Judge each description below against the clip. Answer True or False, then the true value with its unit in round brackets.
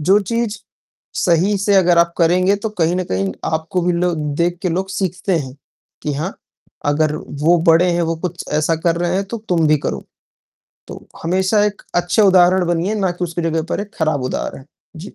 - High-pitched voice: False (175 Hz)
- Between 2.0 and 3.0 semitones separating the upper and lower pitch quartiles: True (2.5 semitones)